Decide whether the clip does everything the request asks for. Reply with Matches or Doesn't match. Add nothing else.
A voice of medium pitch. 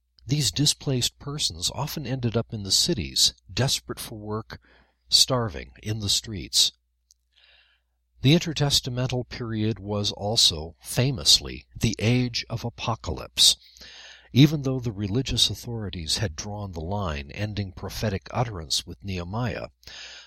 Doesn't match